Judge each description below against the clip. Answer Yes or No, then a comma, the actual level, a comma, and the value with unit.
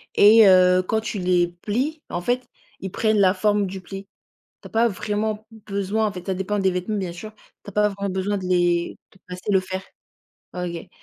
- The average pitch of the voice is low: No, high, 195 Hz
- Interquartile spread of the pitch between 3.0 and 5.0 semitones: No, narrow, 2.6 semitones